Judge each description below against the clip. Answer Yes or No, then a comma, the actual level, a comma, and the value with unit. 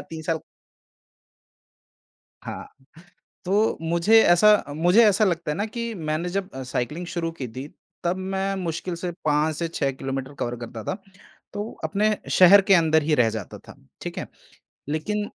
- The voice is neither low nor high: Yes, medium, 170 Hz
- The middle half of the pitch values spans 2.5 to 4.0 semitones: No, average, 4.4 semitones